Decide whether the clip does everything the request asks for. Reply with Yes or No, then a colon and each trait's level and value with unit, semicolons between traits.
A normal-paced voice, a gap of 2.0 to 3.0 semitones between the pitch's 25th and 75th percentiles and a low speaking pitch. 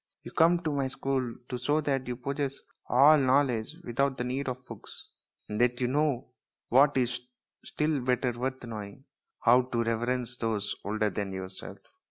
Yes: average, 170 wpm; average, 2.7 semitones; low, 125 Hz